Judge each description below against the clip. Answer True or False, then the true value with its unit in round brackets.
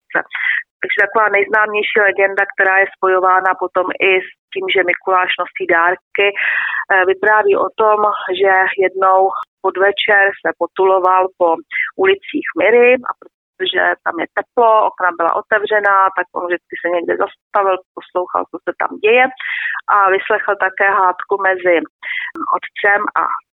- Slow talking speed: False (130 wpm)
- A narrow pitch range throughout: True (2.1 semitones)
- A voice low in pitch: False (195 Hz)